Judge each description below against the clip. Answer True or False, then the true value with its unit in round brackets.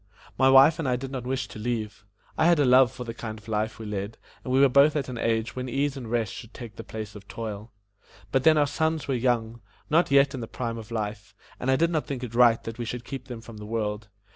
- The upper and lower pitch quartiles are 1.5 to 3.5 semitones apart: True (3.2 semitones)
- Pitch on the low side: True (120 Hz)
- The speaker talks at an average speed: False (270 wpm)